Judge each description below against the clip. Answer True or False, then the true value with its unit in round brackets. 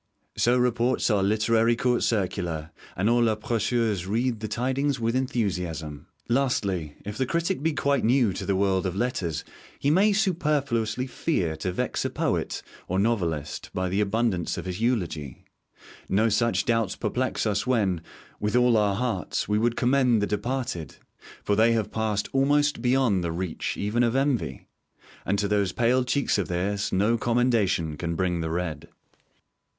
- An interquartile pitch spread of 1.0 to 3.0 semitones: False (4.8 semitones)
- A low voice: True (110 Hz)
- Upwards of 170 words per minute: False (165 wpm)